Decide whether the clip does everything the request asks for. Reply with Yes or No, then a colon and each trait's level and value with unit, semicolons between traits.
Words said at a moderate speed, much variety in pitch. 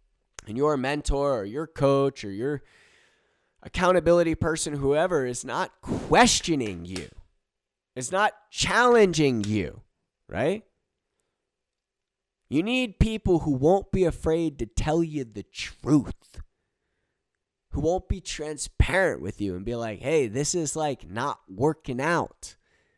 No: slow, 125 wpm; wide, 6.7 semitones